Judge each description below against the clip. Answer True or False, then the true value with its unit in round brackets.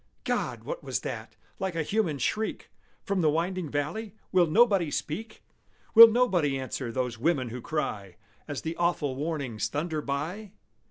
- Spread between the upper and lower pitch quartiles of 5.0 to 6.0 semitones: True (5.4 semitones)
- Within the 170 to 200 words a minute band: False (155 wpm)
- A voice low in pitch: False (160 Hz)